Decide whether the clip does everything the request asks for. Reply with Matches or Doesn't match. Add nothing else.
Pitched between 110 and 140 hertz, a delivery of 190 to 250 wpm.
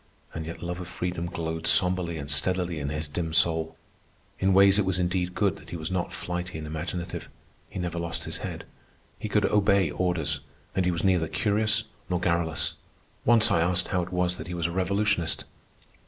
Doesn't match